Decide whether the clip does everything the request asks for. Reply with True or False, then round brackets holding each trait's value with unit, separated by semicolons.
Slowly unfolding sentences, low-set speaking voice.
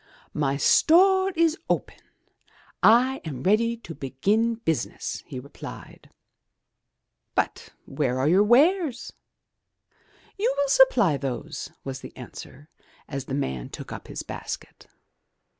False (125 wpm; 200 Hz)